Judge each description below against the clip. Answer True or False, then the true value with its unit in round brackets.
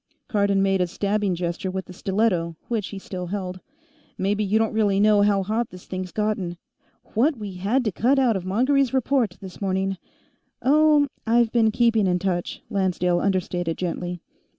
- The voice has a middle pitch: False (200 Hz)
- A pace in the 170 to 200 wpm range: True (175 wpm)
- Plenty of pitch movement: False (3.4 semitones)